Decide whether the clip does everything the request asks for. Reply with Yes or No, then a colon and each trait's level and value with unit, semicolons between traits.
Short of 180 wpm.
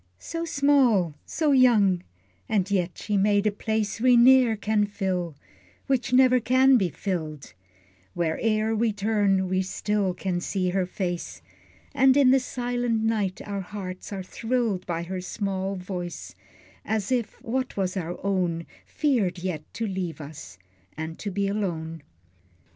Yes: average, 150 wpm